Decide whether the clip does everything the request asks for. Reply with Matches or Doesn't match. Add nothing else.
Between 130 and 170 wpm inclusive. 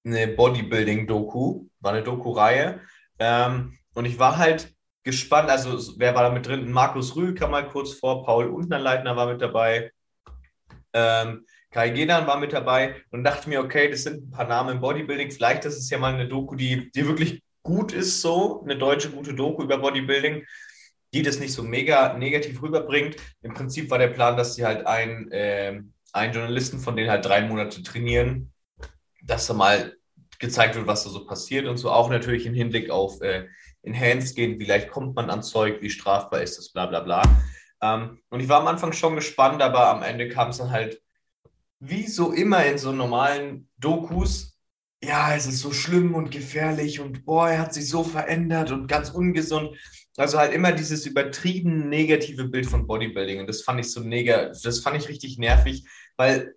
Doesn't match